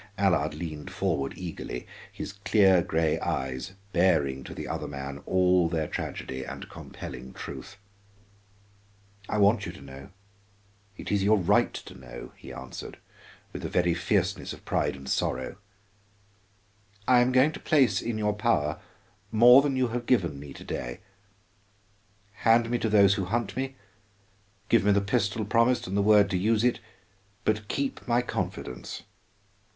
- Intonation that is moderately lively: No, wide, 6.4 semitones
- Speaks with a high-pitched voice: No, low, 100 Hz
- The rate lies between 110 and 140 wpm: No, average, 155 wpm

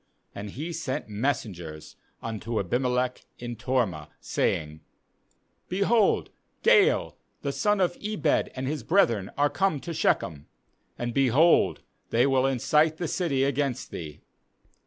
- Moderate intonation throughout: No, wide, 6.1 semitones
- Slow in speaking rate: Yes, slow, 125 wpm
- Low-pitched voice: Yes, low, 130 Hz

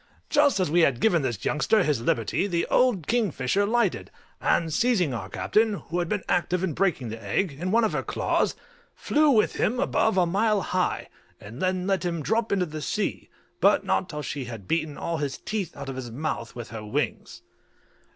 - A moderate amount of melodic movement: No, wide, 6.7 semitones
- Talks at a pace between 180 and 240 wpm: Yes, average, 200 wpm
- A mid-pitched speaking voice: Yes, medium, 175 Hz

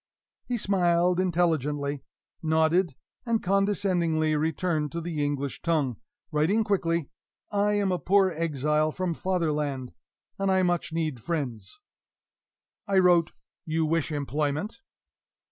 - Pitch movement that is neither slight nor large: Yes, average, 3.6 semitones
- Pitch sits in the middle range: Yes, medium, 165 Hz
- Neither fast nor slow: No, slow, 115 wpm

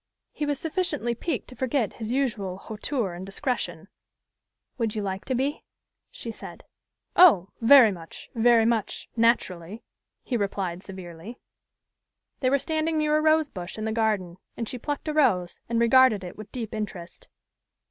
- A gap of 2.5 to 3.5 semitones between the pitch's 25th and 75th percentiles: No, wide, 5.5 semitones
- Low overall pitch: No, high, 230 Hz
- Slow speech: No, average, 160 wpm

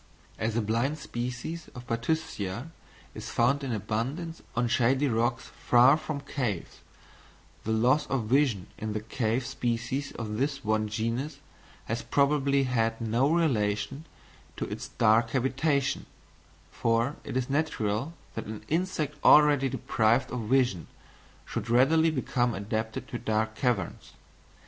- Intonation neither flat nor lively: Yes, average, 4.0 semitones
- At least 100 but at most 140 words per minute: Yes, slow, 135 wpm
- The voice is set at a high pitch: No, low, 120 Hz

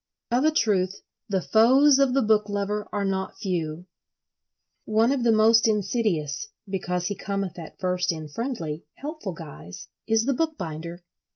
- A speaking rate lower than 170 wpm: Yes, average, 155 wpm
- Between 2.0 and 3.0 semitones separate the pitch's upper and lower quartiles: No, average, 4.3 semitones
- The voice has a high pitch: Yes, high, 205 Hz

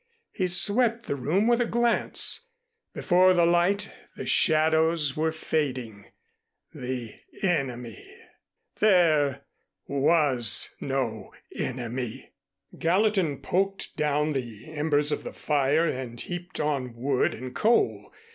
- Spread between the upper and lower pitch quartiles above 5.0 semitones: Yes, wide, 5.5 semitones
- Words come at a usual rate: No, slow, 110 wpm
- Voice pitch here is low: No, medium, 150 Hz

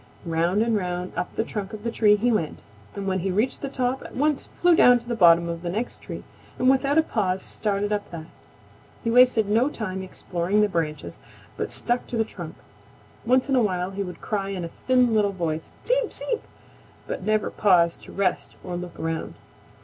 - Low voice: No, high, 205 Hz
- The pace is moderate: No, fast, 210 wpm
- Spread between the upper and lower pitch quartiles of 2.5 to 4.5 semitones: No, average, 5.2 semitones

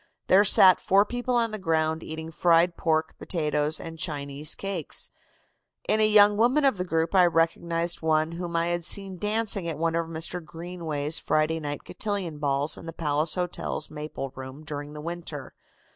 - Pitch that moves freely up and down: No, average, 3.0 semitones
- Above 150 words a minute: Yes, average, 175 wpm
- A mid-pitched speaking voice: Yes, medium, 165 Hz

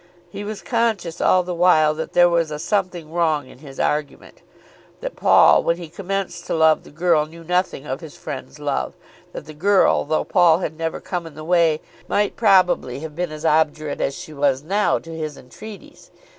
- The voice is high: No, medium, 165 Hz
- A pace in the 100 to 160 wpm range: No, average, 200 wpm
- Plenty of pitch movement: No, average, 2.9 semitones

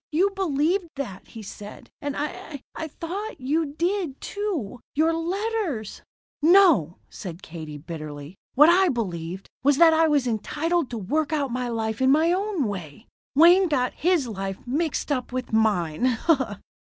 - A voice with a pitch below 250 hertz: No, very high, 280 Hz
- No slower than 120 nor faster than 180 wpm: Yes, average, 155 wpm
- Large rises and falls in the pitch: Yes, wide, 7.6 semitones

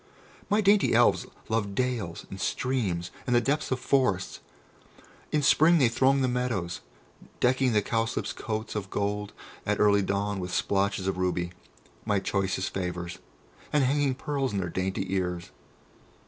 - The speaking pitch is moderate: No, low, 105 Hz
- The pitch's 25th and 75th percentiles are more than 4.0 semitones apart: Yes, average, 5.2 semitones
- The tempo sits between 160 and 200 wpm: No, average, 150 wpm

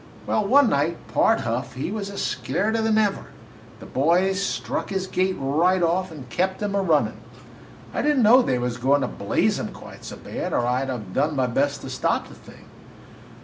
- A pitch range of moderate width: No, wide, 7.2 semitones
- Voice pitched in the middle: Yes, medium, 165 Hz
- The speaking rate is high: Yes, fast, 210 wpm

